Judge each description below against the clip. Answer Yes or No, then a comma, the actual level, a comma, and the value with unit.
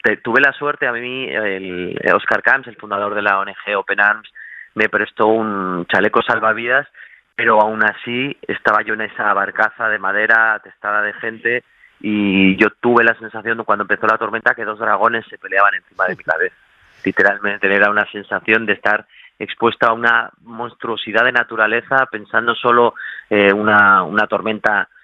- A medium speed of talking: Yes, average, 170 wpm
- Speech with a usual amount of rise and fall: No, narrow, 2.2 semitones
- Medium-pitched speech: No, low, 110 Hz